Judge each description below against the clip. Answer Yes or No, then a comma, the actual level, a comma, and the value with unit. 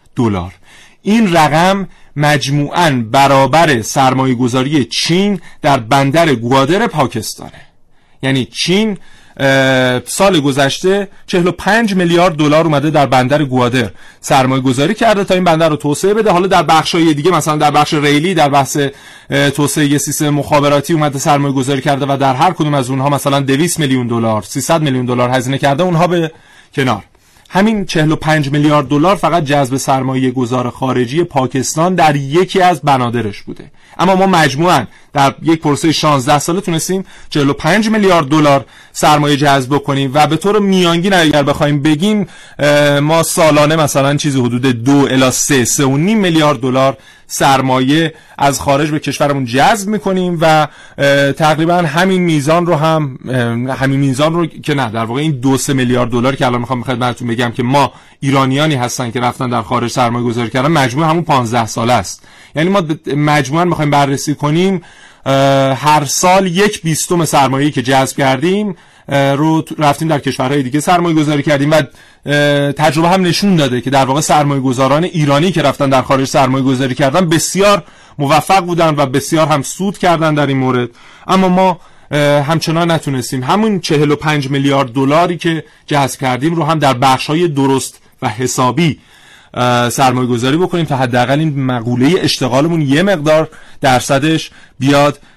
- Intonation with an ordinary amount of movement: Yes, average, 3.5 semitones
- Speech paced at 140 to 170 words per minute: Yes, fast, 155 wpm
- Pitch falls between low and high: Yes, medium, 145 Hz